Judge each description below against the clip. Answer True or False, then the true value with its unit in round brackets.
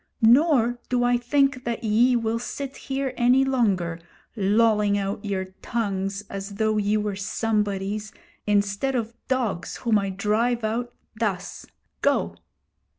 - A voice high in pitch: True (220 Hz)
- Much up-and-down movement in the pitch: False (3.2 semitones)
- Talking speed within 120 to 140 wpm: True (135 wpm)